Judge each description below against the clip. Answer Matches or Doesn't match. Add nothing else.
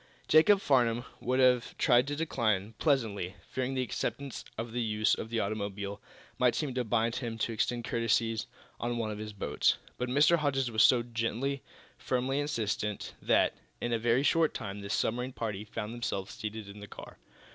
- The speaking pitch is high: Doesn't match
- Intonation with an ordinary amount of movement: Matches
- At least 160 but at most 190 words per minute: Matches